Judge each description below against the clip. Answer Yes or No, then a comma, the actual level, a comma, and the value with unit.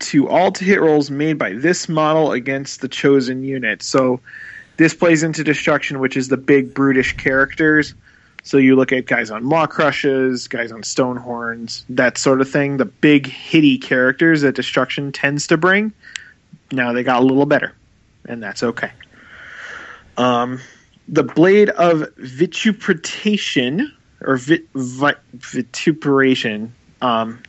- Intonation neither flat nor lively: Yes, average, 3.5 semitones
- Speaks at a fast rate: No, average, 150 wpm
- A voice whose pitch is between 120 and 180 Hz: Yes, low, 135 Hz